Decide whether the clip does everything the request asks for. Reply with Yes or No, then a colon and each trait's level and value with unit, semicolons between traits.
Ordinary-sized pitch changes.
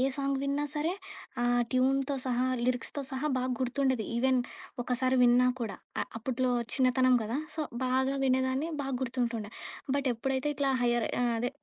No: narrow, 1.6 semitones